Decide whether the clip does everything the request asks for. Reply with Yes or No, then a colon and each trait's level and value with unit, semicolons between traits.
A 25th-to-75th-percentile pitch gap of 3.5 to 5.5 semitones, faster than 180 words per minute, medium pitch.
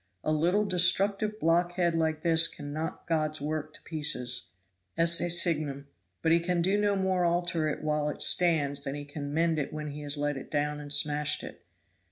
No: average, 2.7 semitones; average, 190 wpm; medium, 155 Hz